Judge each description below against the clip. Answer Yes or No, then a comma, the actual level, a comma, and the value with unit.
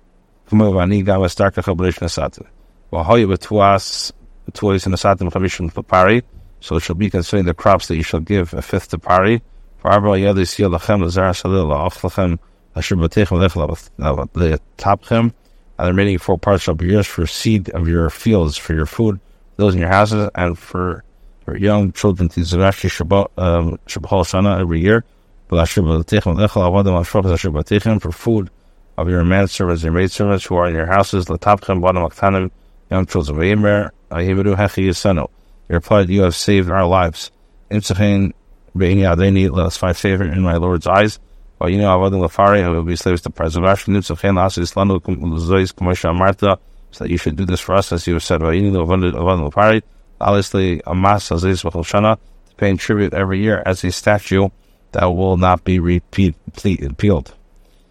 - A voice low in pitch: Yes, very low, 95 Hz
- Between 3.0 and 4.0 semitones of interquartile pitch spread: No, narrow, 2.5 semitones